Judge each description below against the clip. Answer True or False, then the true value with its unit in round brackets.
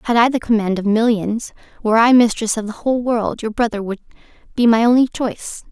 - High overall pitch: True (225 Hz)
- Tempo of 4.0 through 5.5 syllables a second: False (6.1 syllables/s)